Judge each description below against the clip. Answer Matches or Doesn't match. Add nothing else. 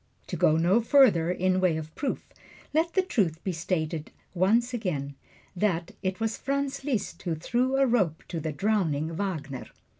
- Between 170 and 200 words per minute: Matches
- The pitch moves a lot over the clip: Matches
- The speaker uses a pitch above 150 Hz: Matches